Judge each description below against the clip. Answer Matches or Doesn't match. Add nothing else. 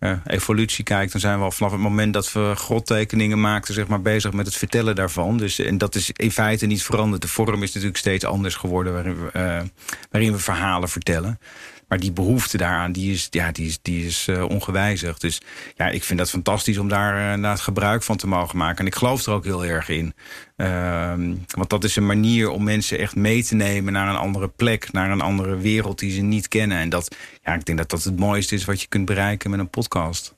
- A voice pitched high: Doesn't match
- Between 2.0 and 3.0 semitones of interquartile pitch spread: Matches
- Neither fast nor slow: Doesn't match